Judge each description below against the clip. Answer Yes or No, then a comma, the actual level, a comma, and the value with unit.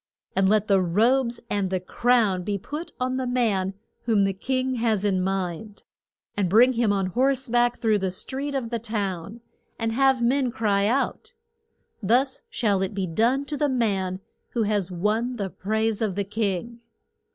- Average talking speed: Yes, average, 175 wpm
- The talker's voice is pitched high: Yes, high, 220 Hz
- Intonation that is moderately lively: Yes, average, 4.1 semitones